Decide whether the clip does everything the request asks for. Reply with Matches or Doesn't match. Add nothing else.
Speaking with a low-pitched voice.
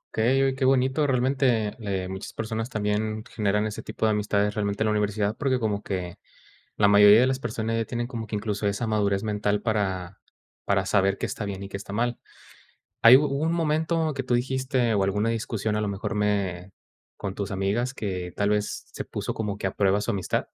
Matches